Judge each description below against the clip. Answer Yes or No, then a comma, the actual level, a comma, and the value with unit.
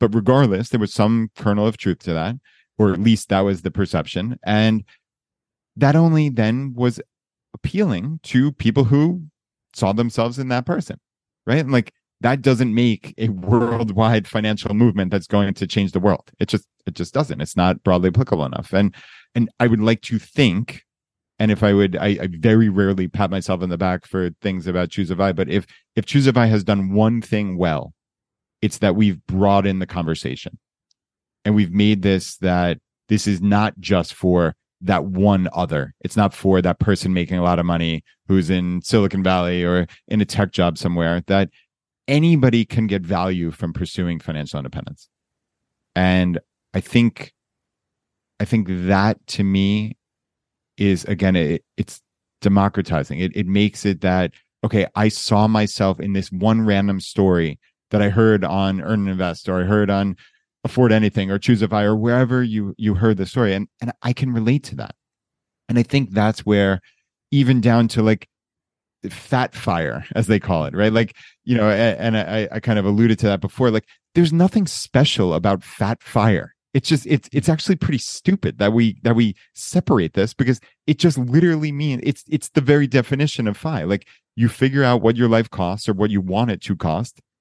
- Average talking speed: Yes, average, 190 wpm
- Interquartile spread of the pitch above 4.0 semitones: No, average, 3.7 semitones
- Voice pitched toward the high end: No, low, 105 Hz